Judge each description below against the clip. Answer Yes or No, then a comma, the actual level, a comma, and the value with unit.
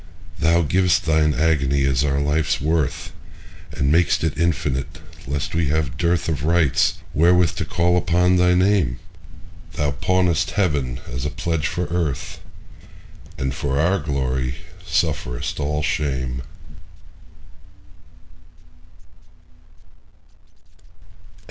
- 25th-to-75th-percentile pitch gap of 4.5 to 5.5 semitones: No, average, 3.6 semitones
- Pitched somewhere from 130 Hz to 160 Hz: No, very low, 80 Hz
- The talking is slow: Yes, slow, 100 wpm